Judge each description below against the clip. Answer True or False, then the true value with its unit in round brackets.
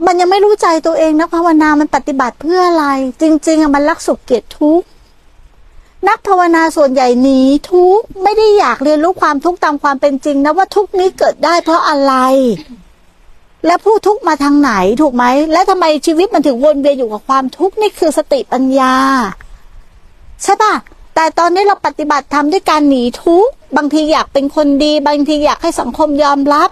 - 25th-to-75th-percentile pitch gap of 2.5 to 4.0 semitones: True (3.7 semitones)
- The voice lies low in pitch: False (310 Hz)